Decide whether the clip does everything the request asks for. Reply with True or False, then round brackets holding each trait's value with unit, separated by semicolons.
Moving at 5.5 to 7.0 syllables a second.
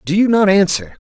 True (5.6 syllables/s)